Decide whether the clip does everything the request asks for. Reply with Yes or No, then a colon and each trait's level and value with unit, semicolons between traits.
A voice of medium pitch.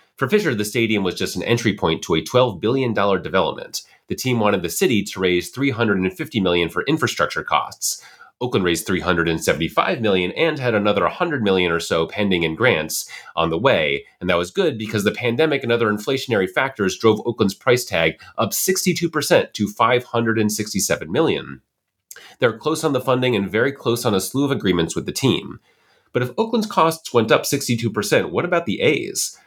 No: low, 110 Hz